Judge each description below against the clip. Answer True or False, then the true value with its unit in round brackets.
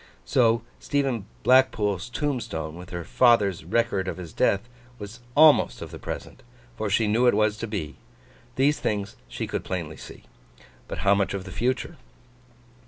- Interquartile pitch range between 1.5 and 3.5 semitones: False (4.2 semitones)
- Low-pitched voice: True (105 Hz)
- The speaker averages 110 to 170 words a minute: True (165 wpm)